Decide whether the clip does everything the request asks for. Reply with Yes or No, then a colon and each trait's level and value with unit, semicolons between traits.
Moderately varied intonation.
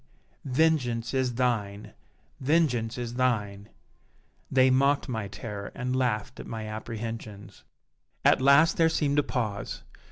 Yes: average, 3.4 semitones